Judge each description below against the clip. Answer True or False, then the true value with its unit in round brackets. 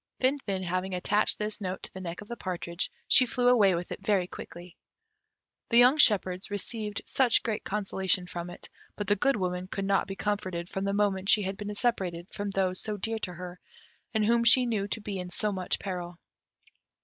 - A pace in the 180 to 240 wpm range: True (200 wpm)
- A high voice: True (195 Hz)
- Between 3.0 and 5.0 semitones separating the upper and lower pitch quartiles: False (2.6 semitones)